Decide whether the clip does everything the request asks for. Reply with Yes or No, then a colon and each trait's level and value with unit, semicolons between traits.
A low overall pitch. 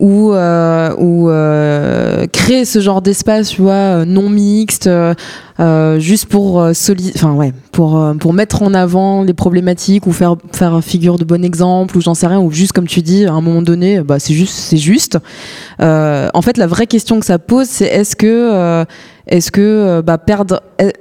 No: medium, 180 Hz